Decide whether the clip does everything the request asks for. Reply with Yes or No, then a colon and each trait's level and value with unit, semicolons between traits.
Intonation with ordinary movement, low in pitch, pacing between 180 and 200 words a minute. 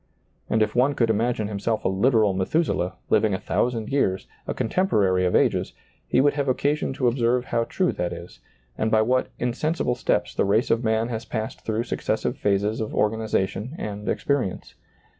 Yes: average, 3.3 semitones; low, 110 Hz; average, 185 wpm